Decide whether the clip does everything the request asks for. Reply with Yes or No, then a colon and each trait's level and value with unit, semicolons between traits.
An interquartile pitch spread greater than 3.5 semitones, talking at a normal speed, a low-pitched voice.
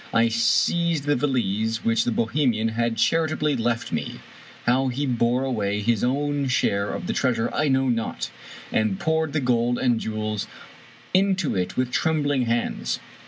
Yes: average, 4.1 semitones; average, 165 wpm; low, 120 Hz